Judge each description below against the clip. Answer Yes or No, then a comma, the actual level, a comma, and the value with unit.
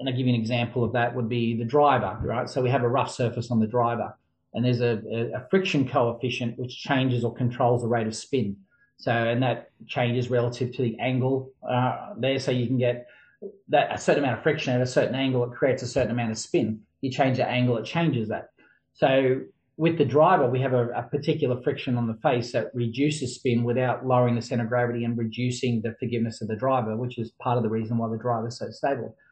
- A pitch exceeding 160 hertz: No, low, 125 Hz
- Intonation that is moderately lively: No, narrow, 1.8 semitones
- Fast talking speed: Yes, fast, 235 wpm